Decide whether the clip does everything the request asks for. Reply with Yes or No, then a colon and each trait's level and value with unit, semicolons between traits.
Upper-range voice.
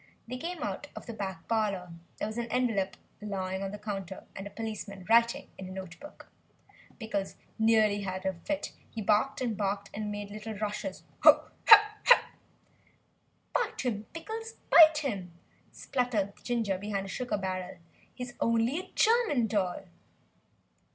Yes: high, 215 Hz